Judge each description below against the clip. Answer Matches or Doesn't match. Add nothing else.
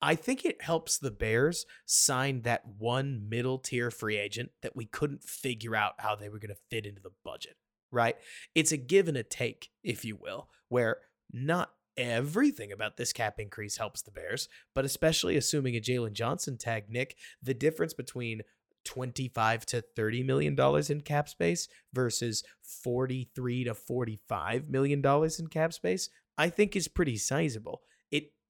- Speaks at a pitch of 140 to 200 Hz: Doesn't match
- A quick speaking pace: Doesn't match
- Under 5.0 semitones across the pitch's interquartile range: Matches